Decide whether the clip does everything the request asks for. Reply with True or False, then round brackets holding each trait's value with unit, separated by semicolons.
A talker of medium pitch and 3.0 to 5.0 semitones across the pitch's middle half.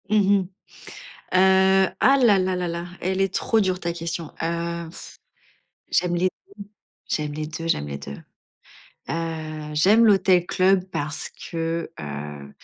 True (170 Hz; 3.3 semitones)